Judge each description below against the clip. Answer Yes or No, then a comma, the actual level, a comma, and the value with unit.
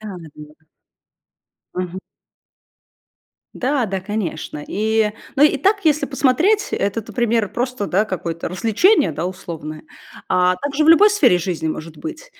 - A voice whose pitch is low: No, high, 215 Hz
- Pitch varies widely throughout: Yes, wide, 8.1 semitones